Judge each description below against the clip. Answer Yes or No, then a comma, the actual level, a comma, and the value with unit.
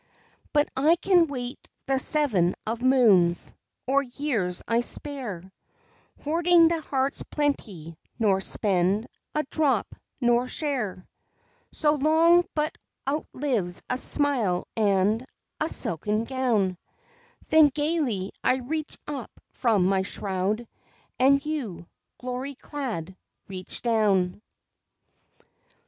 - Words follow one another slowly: Yes, slow, 105 wpm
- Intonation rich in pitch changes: Yes, wide, 6.9 semitones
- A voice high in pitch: Yes, very high, 250 Hz